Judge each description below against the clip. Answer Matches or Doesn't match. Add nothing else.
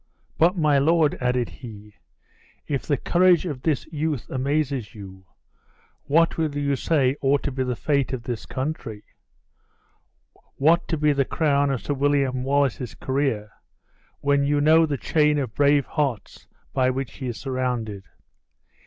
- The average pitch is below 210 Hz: Matches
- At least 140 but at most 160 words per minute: Matches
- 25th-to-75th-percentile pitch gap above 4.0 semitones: Doesn't match